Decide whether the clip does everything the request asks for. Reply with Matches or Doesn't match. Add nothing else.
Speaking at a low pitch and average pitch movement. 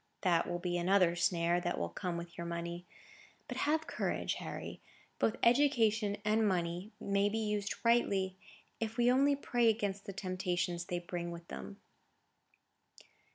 Doesn't match